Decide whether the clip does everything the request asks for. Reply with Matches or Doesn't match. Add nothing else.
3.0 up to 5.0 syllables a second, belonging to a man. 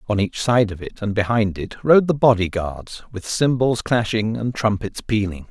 Matches